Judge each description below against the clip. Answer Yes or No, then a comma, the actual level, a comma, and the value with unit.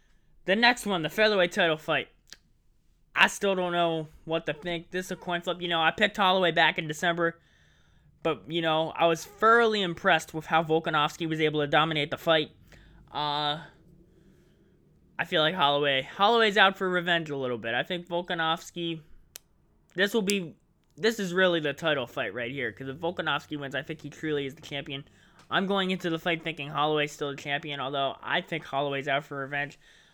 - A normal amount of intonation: Yes, average, 3.6 semitones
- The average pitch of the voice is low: No, medium, 160 Hz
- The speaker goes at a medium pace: Yes, average, 195 wpm